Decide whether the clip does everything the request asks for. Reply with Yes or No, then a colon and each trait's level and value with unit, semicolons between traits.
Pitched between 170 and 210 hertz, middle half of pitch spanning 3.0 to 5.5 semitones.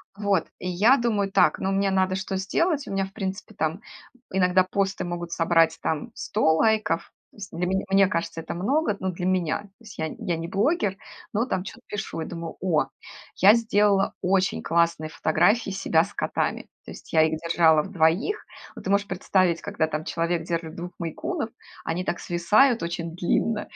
Yes: medium, 185 Hz; average, 3.3 semitones